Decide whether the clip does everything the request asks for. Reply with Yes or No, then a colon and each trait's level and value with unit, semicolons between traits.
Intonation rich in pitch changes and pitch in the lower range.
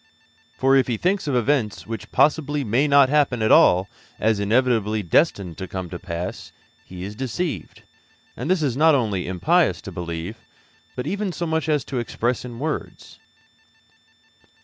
Yes: wide, 6.5 semitones; low, 120 Hz